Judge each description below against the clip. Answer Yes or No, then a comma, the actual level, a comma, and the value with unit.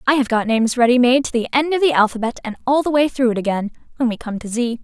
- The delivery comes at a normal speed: No, fast, 300 wpm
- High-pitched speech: Yes, high, 245 Hz